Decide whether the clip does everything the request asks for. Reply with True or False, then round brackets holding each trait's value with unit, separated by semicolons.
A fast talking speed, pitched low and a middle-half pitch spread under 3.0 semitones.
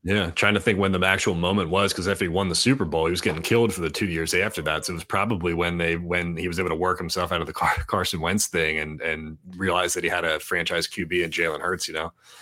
True (290 wpm; 90 Hz; 2.6 semitones)